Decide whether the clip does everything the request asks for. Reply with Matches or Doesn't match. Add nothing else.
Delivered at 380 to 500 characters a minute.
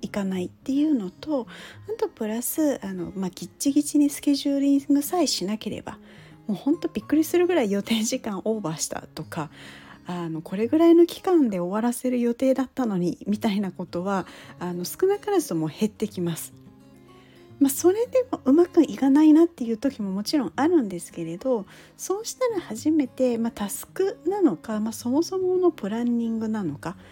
Matches